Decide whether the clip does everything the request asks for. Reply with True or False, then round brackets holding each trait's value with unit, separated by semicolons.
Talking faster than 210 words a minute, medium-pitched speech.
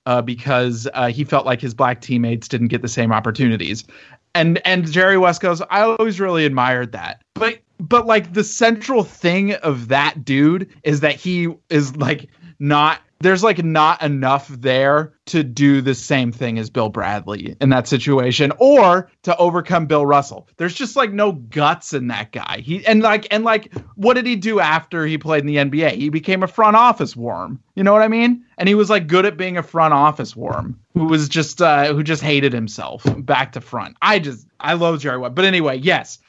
False (205 wpm; 150 Hz)